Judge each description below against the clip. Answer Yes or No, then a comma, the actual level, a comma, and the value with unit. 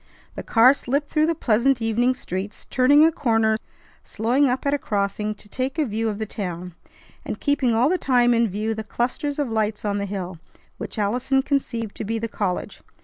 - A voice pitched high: Yes, high, 230 Hz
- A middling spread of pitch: Yes, average, 4.2 semitones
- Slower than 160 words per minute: No, fast, 205 wpm